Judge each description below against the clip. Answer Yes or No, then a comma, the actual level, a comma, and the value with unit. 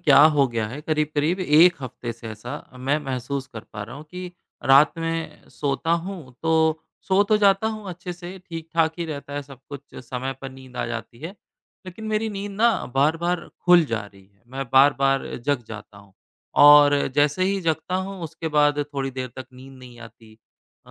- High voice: No, medium, 145 Hz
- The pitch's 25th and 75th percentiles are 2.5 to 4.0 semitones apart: No, average, 4.8 semitones